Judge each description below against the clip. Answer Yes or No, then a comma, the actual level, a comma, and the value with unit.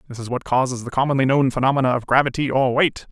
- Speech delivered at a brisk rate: Yes, fast, 230 wpm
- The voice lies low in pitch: Yes, low, 130 Hz